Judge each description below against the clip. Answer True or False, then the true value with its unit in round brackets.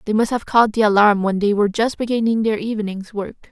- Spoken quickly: True (240 wpm)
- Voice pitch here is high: True (215 Hz)